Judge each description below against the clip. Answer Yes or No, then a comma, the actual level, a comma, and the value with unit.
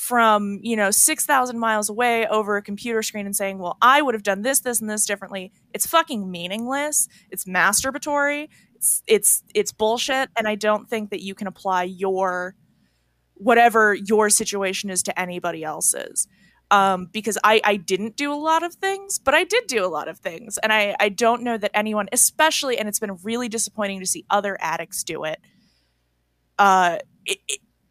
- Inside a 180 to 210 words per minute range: Yes, average, 185 wpm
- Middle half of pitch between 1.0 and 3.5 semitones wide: No, average, 4.2 semitones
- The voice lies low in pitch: No, high, 210 Hz